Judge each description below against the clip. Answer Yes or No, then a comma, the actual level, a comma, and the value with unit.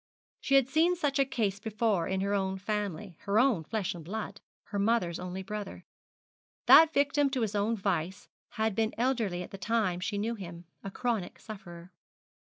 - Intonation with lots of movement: No, average, 3.7 semitones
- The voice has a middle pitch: No, high, 210 Hz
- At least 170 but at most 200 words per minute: Yes, average, 180 wpm